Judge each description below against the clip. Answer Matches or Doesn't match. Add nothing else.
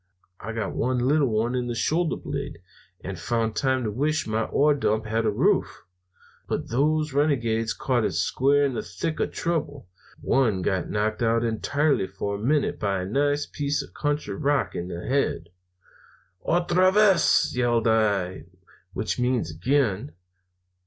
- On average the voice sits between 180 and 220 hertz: Doesn't match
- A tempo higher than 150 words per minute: Matches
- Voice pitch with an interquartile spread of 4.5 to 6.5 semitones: Matches